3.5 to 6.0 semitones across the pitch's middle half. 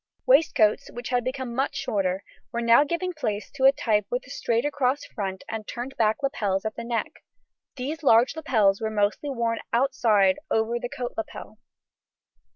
Yes: average, 3.9 semitones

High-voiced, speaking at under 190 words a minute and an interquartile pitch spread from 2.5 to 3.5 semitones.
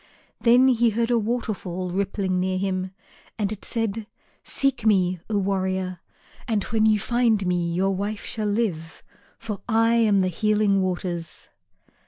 Yes: high, 200 Hz; average, 150 wpm; average, 3.2 semitones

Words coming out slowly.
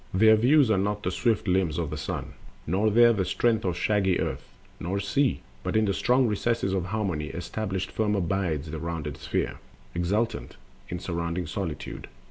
No: average, 180 wpm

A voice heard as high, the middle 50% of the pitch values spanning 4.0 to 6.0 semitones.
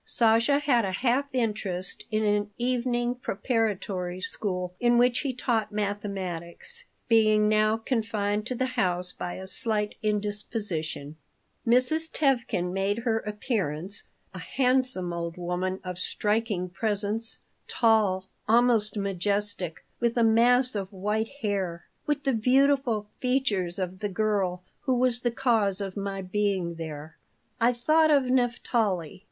Yes: high, 210 Hz; average, 4.3 semitones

